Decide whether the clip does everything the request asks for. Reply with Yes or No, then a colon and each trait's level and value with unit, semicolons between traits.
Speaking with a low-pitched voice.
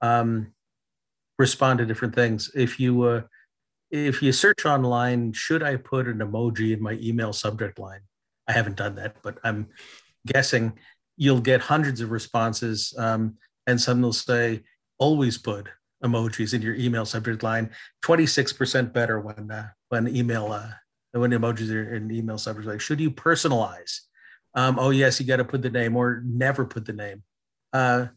Yes: low, 120 Hz